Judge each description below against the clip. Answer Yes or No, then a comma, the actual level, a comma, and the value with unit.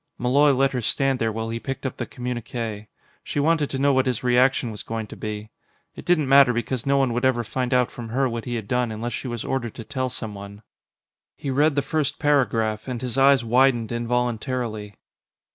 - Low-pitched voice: Yes, low, 125 Hz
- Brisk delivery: Yes, fast, 210 wpm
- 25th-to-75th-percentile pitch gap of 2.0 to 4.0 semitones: Yes, average, 2.9 semitones